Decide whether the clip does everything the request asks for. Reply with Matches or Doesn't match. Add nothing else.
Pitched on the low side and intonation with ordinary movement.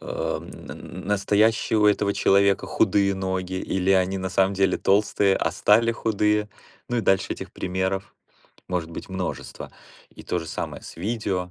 Doesn't match